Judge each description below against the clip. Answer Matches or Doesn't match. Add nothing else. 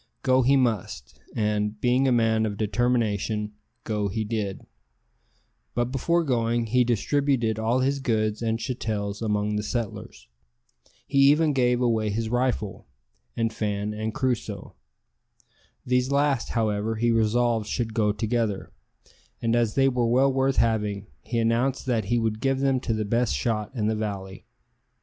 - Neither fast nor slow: Matches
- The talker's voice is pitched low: Matches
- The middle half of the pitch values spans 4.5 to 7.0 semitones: Doesn't match